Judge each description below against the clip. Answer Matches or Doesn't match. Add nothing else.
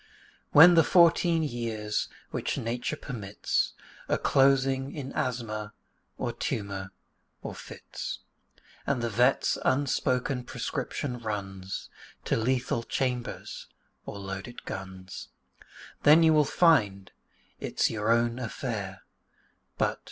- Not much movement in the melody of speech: Doesn't match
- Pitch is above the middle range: Doesn't match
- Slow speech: Matches